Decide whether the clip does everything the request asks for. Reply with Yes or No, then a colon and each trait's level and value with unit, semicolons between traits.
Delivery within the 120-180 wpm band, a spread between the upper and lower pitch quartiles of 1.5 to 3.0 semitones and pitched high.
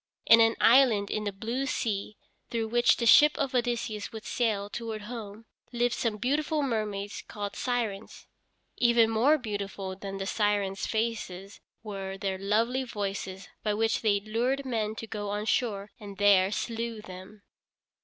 Yes: average, 155 wpm; average, 2.7 semitones; high, 215 Hz